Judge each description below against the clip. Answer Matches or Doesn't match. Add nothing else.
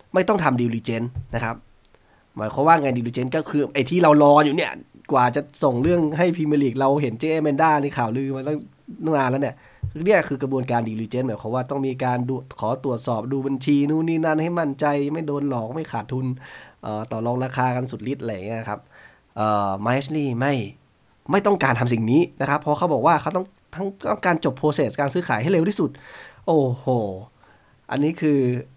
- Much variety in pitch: Doesn't match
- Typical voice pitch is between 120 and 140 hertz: Matches